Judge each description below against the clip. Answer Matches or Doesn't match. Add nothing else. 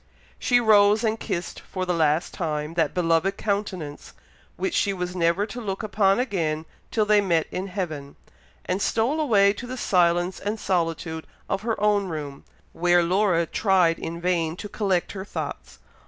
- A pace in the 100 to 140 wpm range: Doesn't match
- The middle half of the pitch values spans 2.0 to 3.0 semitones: Doesn't match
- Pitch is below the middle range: Doesn't match